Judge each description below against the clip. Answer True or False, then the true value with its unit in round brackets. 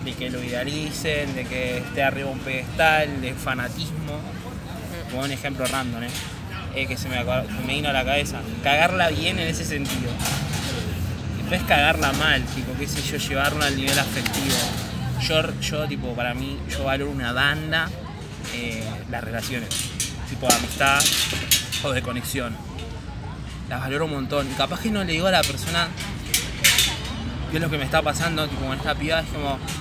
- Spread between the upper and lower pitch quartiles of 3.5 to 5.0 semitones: True (4.1 semitones)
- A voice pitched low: True (130 Hz)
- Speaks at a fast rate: False (175 wpm)